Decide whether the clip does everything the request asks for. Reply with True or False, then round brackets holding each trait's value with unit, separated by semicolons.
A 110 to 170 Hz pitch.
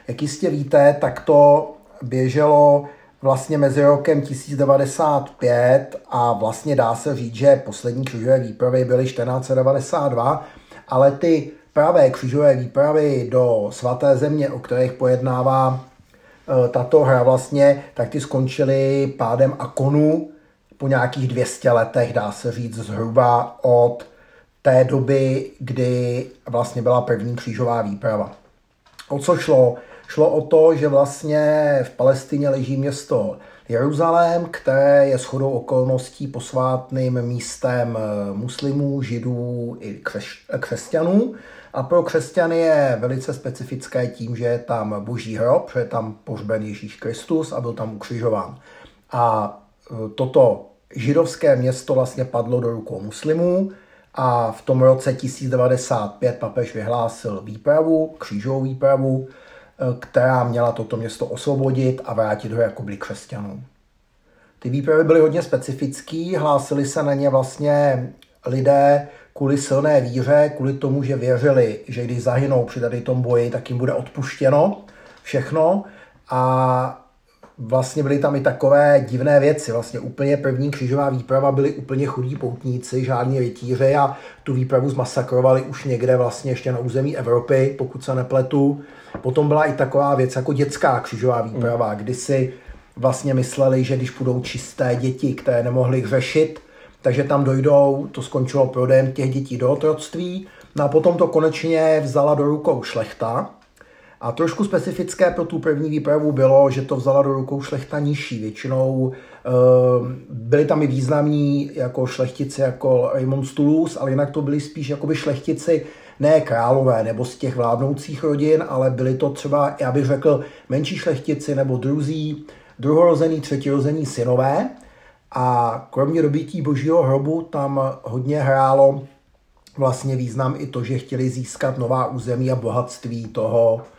True (135 Hz)